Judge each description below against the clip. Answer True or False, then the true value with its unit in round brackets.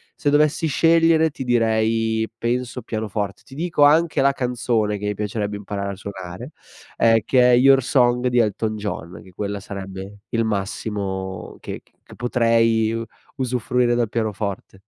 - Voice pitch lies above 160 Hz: False (115 Hz)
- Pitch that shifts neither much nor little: True (3.4 semitones)